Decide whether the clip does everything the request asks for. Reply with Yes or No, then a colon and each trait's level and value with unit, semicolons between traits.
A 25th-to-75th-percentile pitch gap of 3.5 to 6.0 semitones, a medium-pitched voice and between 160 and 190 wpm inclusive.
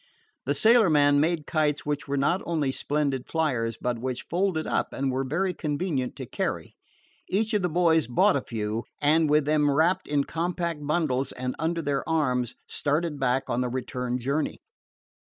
Yes: average, 3.9 semitones; medium, 145 Hz; average, 170 wpm